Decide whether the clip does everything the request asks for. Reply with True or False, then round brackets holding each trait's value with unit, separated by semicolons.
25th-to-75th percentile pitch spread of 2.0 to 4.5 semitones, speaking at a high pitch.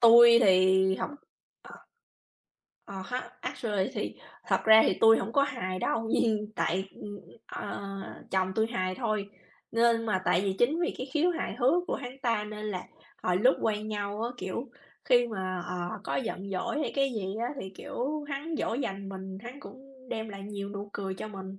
True (4.0 semitones; 215 Hz)